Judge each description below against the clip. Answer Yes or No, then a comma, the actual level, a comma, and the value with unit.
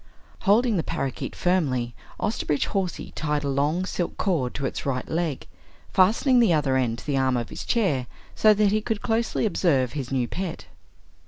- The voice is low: No, medium, 155 Hz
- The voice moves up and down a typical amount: No, wide, 7.0 semitones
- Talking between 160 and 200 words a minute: Yes, average, 180 wpm